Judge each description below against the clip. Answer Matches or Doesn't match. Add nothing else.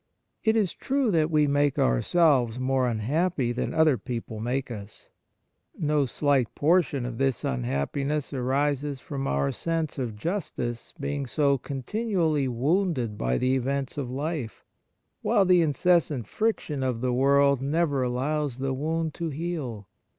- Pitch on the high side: Doesn't match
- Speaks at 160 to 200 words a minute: Doesn't match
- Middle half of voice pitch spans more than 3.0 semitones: Matches